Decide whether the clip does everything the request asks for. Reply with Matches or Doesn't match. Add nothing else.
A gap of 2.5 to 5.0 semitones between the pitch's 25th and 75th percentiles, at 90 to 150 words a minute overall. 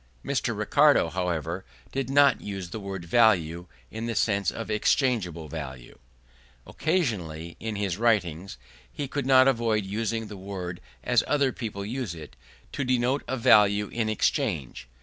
Doesn't match